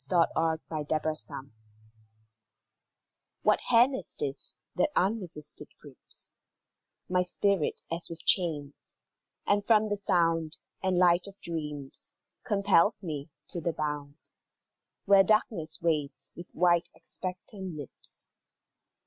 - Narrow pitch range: No, average, 4.1 semitones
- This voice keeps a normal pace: No, slow, 110 wpm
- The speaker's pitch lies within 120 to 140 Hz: No, medium, 170 Hz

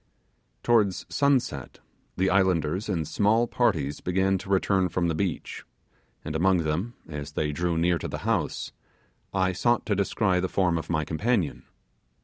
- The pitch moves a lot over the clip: No, average, 3.6 semitones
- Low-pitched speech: Yes, very low, 90 Hz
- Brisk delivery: No, average, 155 wpm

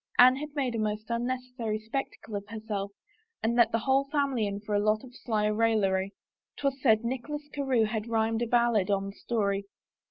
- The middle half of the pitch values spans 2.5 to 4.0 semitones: Yes, average, 3.1 semitones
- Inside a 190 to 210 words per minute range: Yes, average, 195 wpm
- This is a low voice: No, high, 225 Hz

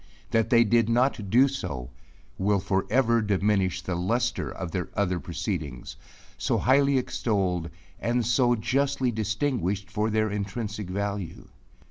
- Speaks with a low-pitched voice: Yes, low, 105 Hz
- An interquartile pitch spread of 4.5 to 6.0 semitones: No, average, 4.1 semitones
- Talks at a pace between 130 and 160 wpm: Yes, slow, 135 wpm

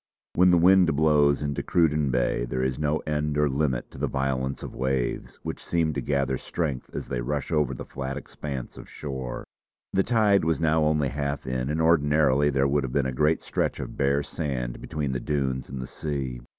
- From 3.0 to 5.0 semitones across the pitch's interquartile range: No, narrow, 2.6 semitones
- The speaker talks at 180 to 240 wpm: Yes, fast, 205 wpm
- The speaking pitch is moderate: No, very low, 70 Hz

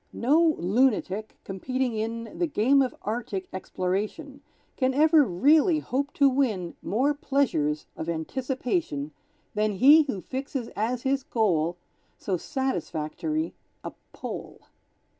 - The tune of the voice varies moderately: No, wide, 6.5 semitones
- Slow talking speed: Yes, slow, 120 wpm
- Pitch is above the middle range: Yes, very high, 250 Hz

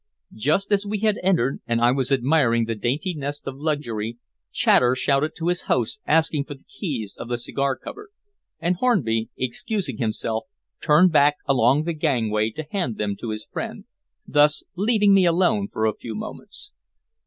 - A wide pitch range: Yes, wide, 6.6 semitones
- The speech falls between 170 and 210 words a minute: Yes, average, 175 wpm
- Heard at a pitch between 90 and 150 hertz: Yes, medium, 140 Hz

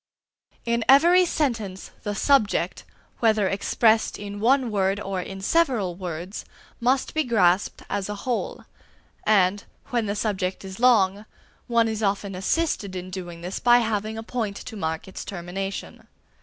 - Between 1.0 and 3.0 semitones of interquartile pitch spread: No, average, 3.6 semitones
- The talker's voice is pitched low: No, high, 205 Hz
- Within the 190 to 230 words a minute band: No, average, 150 wpm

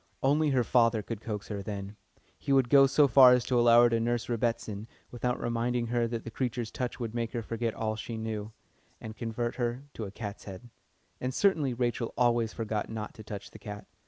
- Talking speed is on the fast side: Yes, fast, 215 wpm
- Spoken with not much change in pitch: Yes, narrow, 2.0 semitones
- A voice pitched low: Yes, low, 115 Hz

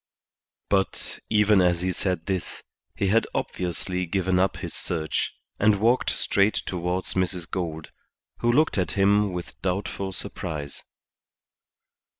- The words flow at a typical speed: No, slow, 130 wpm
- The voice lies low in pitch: Yes, very low, 95 Hz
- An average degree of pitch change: No, narrow, 2.2 semitones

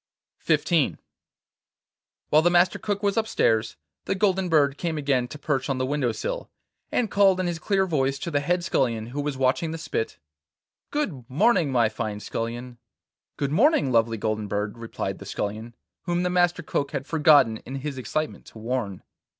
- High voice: No, medium, 145 Hz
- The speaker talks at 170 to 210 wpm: Yes, average, 175 wpm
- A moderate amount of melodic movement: No, wide, 6.6 semitones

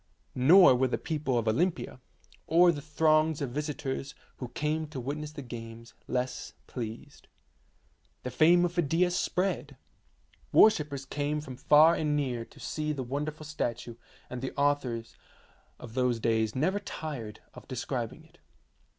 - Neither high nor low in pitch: Yes, medium, 145 Hz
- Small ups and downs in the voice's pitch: No, average, 3.8 semitones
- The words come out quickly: No, average, 145 wpm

